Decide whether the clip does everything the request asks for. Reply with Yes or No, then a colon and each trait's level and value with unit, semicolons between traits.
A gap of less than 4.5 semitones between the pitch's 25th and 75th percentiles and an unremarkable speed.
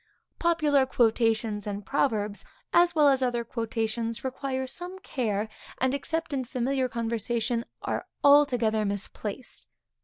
No: average, 3.8 semitones; slow, 120 wpm